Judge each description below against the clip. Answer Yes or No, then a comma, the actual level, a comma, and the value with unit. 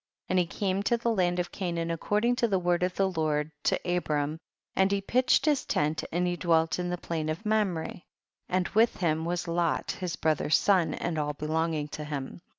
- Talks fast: Yes, fast, 210 wpm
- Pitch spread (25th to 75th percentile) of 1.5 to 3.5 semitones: Yes, average, 3.1 semitones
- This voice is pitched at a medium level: Yes, medium, 175 Hz